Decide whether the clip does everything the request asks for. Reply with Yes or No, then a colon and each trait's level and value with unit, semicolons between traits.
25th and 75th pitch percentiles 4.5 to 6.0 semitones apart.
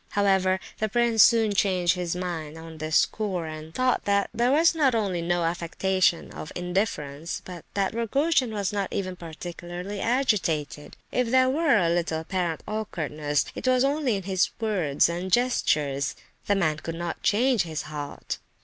Yes: average, 5.1 semitones